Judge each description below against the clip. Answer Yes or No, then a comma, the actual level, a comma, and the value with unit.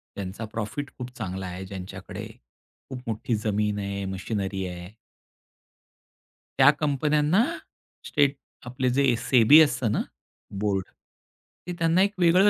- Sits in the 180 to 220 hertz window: No, low, 115 Hz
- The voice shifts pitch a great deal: Yes, wide, 6.6 semitones